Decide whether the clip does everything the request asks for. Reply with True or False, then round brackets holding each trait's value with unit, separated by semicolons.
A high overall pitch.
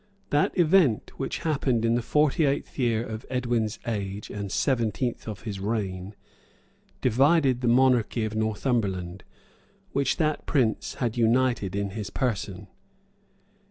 False (115 Hz)